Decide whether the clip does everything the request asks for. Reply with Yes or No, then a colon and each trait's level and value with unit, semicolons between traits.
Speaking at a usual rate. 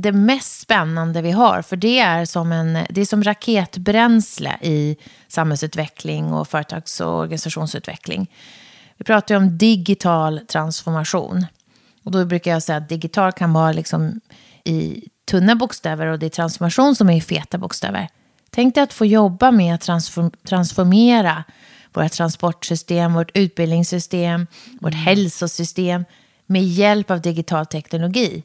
Yes: average, 140 wpm